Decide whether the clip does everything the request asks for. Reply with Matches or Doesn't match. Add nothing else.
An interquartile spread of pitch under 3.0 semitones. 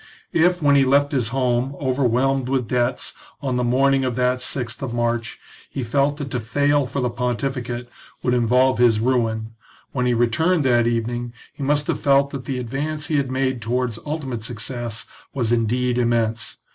Matches